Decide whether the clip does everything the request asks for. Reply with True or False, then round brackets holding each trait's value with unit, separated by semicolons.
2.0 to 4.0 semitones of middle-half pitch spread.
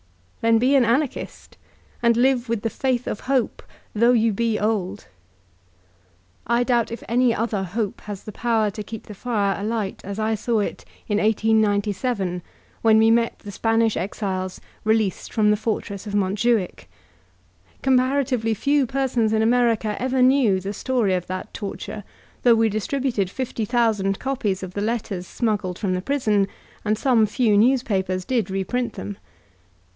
True (2.9 semitones)